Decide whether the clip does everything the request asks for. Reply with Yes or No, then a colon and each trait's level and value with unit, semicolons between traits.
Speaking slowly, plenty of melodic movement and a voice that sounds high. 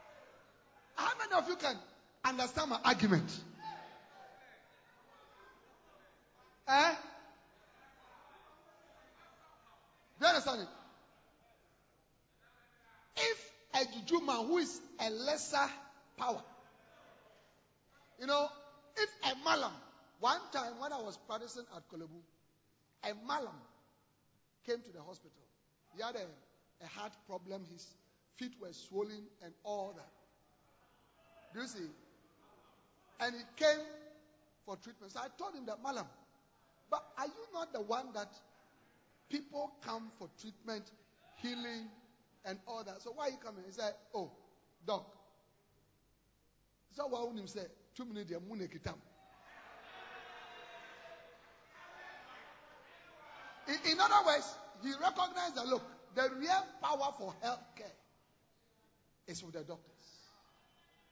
Yes: slow, 115 wpm; wide, 6.2 semitones; high, 240 Hz